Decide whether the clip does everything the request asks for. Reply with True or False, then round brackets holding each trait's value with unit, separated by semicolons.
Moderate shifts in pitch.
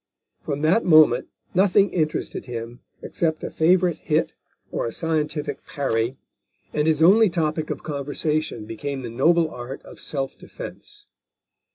True (3.8 semitones)